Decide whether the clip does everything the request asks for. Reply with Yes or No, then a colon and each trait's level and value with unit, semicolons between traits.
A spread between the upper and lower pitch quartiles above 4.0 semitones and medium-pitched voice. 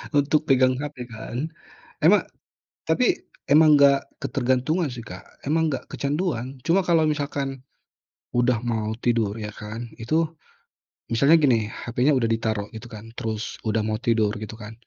No: average, 4.5 semitones; low, 125 Hz